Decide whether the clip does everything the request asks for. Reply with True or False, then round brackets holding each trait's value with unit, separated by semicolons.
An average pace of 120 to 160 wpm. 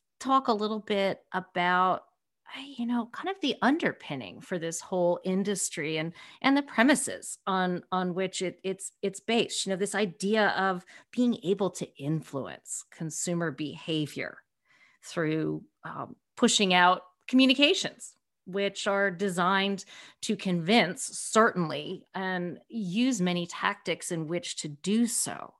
True (135 wpm)